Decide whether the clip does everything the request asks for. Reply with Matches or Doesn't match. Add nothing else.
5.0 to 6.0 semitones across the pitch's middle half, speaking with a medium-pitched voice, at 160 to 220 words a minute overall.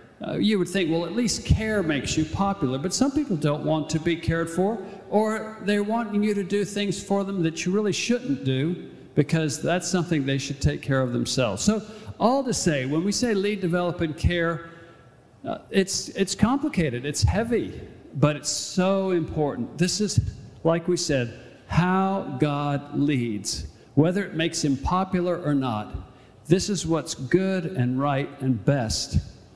Matches